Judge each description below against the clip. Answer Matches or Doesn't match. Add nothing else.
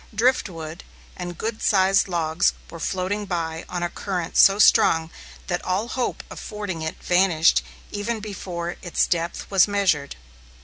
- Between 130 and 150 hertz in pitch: Doesn't match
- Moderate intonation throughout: Matches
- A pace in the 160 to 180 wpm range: Doesn't match